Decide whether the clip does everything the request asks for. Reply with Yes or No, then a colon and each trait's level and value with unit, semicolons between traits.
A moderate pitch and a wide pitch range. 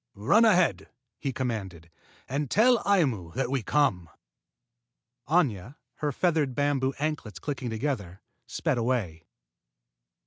No: low, 130 Hz; wide, 6.0 semitones